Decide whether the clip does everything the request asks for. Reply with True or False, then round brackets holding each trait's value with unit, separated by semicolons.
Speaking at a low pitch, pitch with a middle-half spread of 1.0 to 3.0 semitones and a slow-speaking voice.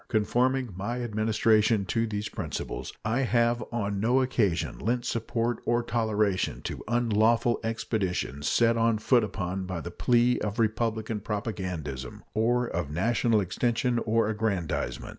True (110 Hz; 2.6 semitones; 130 wpm)